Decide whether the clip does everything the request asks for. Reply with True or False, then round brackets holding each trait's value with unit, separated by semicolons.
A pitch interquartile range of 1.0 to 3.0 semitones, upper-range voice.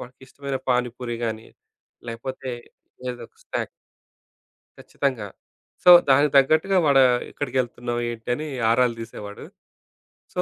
False (2.6 semitones; 125 Hz)